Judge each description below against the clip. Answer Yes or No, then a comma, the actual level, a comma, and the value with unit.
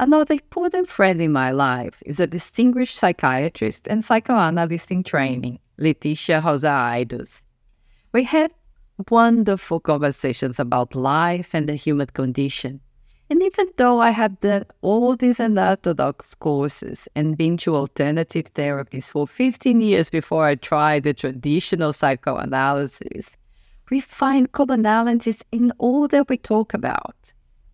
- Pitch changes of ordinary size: No, wide, 8.5 semitones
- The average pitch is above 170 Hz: No, medium, 165 Hz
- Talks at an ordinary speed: No, slow, 130 wpm